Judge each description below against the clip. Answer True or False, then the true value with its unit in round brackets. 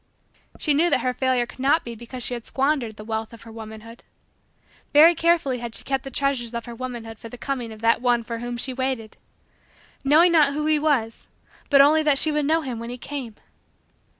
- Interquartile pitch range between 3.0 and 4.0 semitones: True (3.7 semitones)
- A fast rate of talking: True (220 wpm)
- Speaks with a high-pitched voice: True (255 Hz)